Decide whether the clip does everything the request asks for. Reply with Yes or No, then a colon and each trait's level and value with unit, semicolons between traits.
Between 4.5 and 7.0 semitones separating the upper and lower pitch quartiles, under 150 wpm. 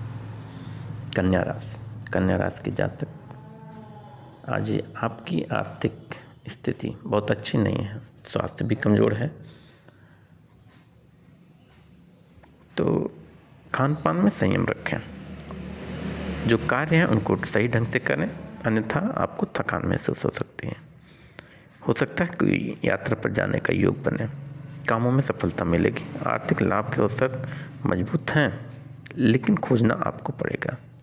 No: average, 4.0 semitones; average, 120 wpm